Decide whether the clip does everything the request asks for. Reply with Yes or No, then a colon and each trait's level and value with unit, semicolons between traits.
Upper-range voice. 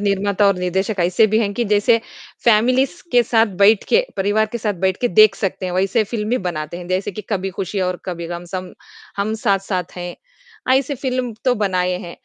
Yes: high, 200 Hz